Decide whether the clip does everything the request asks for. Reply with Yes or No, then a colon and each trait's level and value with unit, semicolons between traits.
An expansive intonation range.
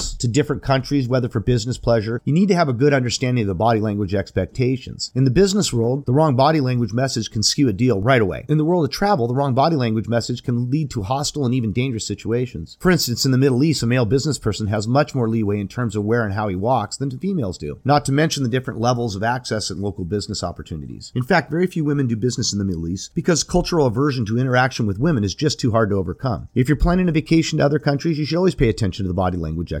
No: average, 4.9 semitones